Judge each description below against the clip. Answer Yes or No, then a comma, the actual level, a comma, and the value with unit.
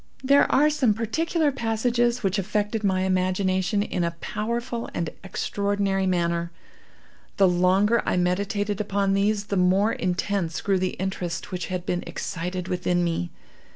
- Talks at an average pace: Yes, average, 145 wpm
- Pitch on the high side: Yes, high, 195 Hz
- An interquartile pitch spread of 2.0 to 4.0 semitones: Yes, average, 2.9 semitones